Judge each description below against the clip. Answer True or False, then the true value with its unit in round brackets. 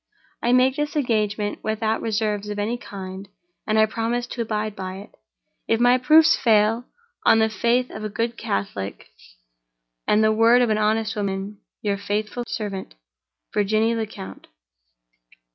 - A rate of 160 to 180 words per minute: False (145 wpm)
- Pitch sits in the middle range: False (215 Hz)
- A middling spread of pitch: False (2.3 semitones)